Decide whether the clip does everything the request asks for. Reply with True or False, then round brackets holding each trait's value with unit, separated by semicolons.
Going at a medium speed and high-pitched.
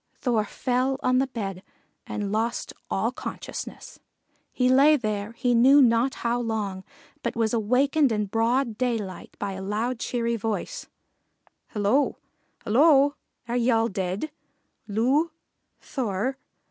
False (130 wpm; 235 Hz)